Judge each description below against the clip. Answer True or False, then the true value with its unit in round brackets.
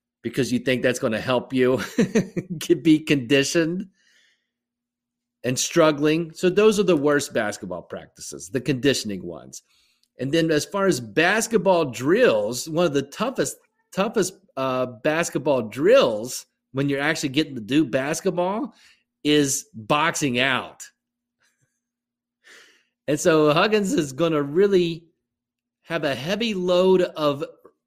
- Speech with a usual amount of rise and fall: False (5.9 semitones)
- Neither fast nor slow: False (130 wpm)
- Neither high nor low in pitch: True (155 Hz)